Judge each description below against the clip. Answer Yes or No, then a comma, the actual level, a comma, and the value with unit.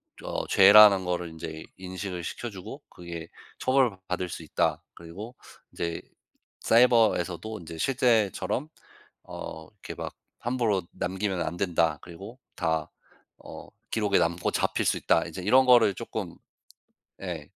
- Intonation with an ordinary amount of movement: Yes, average, 4.5 semitones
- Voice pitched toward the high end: No, very low, 95 Hz